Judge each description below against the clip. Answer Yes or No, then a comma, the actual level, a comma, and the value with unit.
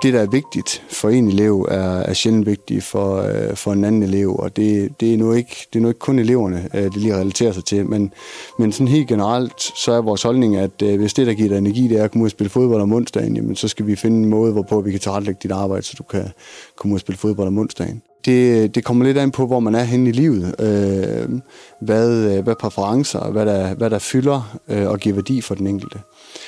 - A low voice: Yes, low, 110 Hz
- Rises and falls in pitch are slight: No, average, 3.2 semitones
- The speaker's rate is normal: No, fast, 240 wpm